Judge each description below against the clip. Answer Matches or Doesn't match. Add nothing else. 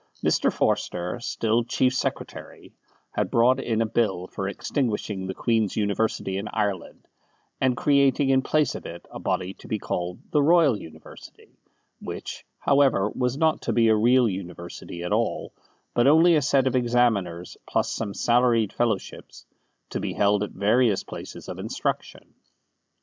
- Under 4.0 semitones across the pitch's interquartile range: Doesn't match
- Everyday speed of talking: Matches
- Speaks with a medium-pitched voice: Doesn't match